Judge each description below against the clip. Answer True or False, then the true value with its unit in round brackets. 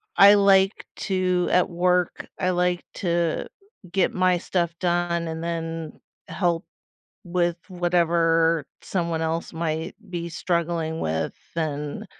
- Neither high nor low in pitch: True (170 Hz)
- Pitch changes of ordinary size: False (1.6 semitones)